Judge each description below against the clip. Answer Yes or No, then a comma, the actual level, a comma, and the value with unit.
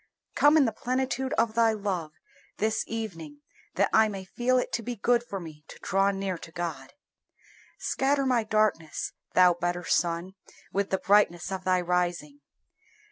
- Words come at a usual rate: Yes, average, 165 wpm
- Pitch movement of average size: Yes, average, 4.6 semitones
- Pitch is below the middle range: No, high, 195 Hz